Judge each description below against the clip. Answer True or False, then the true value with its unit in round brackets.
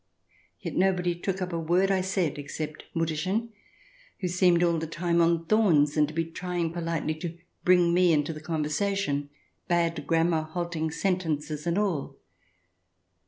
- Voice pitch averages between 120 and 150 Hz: False (170 Hz)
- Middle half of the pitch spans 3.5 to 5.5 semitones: False (2.4 semitones)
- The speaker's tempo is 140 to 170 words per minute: True (155 wpm)